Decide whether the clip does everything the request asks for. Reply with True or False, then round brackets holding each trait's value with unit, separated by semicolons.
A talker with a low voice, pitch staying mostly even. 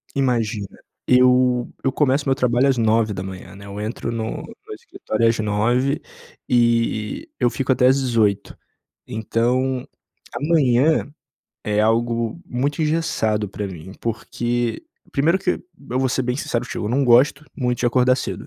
False (120 Hz; 3.0 semitones)